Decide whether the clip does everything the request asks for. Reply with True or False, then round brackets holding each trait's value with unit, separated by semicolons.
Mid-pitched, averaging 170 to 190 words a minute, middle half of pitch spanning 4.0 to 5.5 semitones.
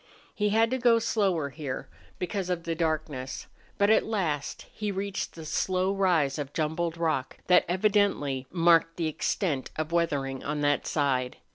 False (165 Hz; 160 wpm; 5.0 semitones)